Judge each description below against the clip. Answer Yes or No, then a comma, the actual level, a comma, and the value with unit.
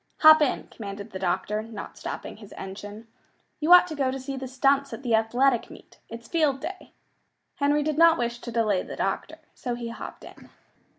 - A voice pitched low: No, high, 245 Hz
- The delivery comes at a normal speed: Yes, average, 195 wpm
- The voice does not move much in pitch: No, average, 4.3 semitones